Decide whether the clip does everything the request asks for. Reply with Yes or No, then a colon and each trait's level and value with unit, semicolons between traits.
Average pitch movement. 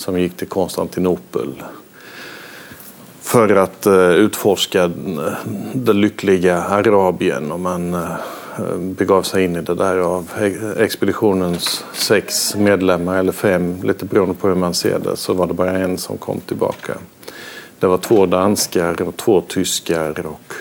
No: narrow, 1.3 semitones